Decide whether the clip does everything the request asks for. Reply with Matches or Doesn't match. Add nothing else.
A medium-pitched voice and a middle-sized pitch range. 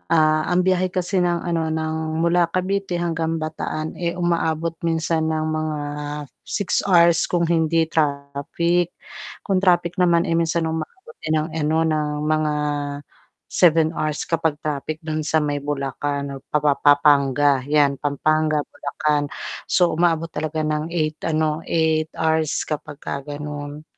Doesn't match